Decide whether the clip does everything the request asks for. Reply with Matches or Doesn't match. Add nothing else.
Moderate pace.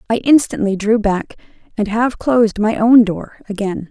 Matches